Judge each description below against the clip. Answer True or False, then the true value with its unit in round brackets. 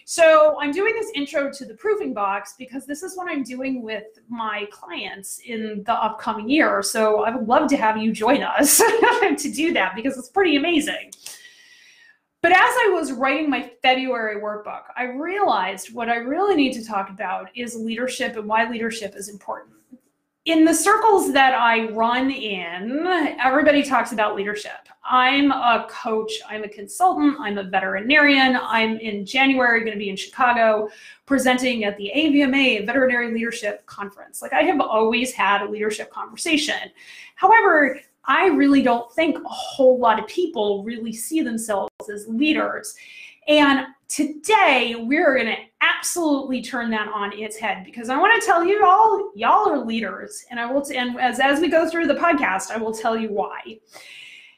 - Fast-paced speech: False (175 wpm)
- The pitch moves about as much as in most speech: False (6.1 semitones)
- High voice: True (255 Hz)